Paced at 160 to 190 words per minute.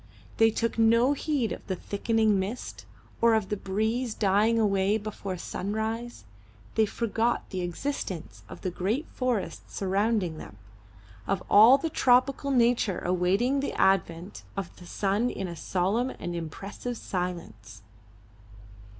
No: slow, 135 wpm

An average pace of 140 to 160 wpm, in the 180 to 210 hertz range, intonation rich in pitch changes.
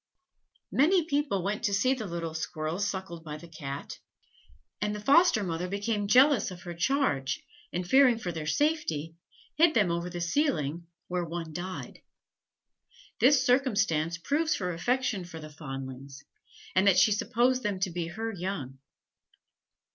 Yes: average, 155 wpm; medium, 185 Hz; wide, 6.8 semitones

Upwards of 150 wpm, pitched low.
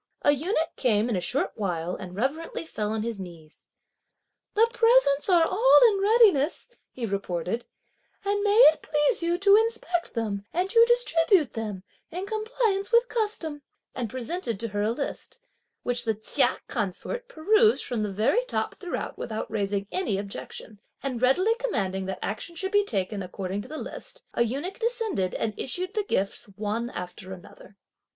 No: average, 170 wpm; very high, 270 Hz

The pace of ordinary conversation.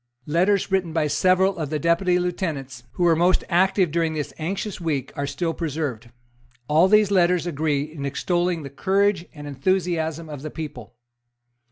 Yes: average, 165 wpm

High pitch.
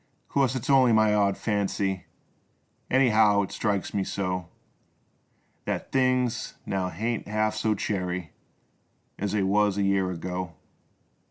No: low, 105 Hz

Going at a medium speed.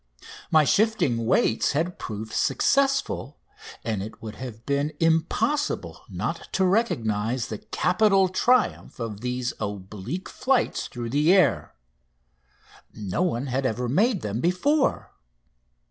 No: slow, 120 wpm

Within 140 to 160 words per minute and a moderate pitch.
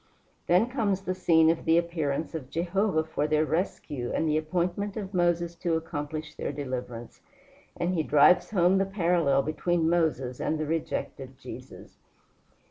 Yes: average, 155 wpm; medium, 165 Hz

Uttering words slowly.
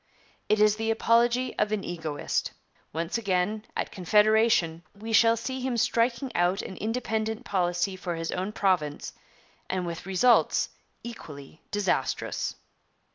Yes: slow, 130 wpm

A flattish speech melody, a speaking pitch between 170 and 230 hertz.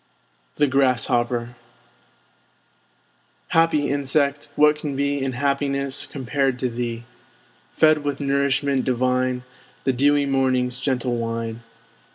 No: narrow, 2.2 semitones; low, 135 Hz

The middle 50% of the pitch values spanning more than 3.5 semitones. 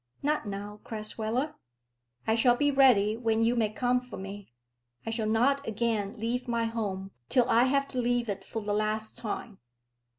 No: narrow, 2.6 semitones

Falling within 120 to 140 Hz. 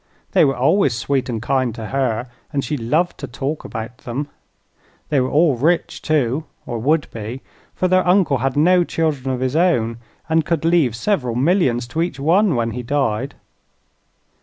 Yes: low, 135 Hz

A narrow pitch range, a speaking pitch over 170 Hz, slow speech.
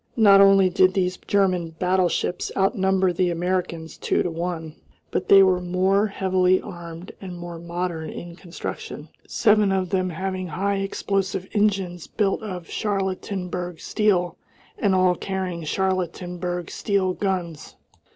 Yes: narrow, 1.7 semitones; medium, 185 Hz; slow, 130 wpm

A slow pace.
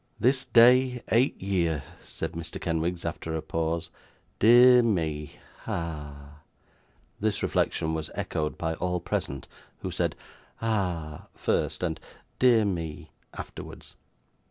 Yes: slow, 115 wpm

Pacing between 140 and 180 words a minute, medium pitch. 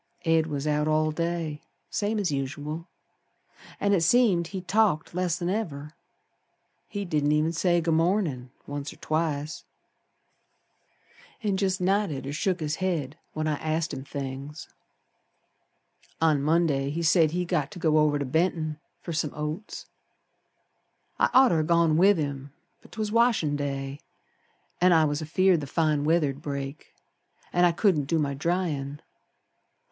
Yes: average, 150 wpm; medium, 155 Hz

